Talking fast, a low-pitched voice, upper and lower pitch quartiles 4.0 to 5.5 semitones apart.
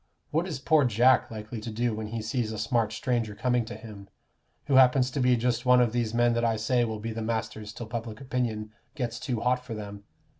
No: fast, 230 wpm; low, 115 Hz; narrow, 2.4 semitones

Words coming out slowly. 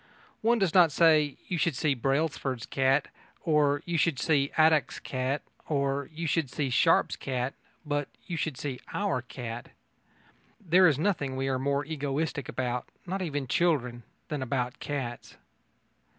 No: average, 150 wpm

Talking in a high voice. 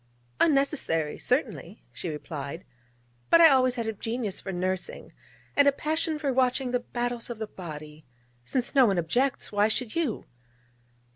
Yes: high, 240 Hz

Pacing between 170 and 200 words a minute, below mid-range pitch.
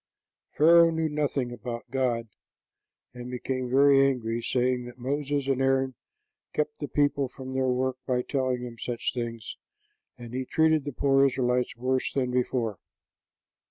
No: average, 150 wpm; low, 130 Hz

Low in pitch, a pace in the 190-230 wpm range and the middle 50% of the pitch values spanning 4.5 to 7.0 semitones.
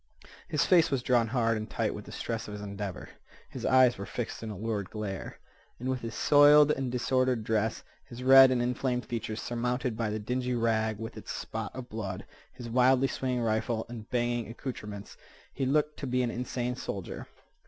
No: low, 120 Hz; average, 195 wpm; average, 2.7 semitones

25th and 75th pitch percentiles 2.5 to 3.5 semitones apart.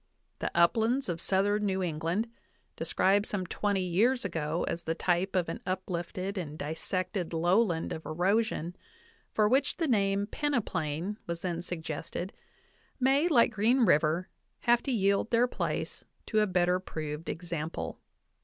No: average, 4.2 semitones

